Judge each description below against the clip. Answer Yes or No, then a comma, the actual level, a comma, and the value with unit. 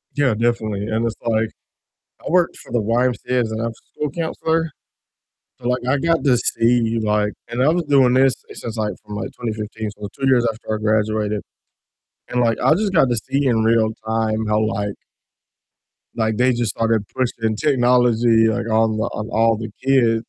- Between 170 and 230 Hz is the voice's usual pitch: No, low, 115 Hz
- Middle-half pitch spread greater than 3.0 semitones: No, narrow, 2.5 semitones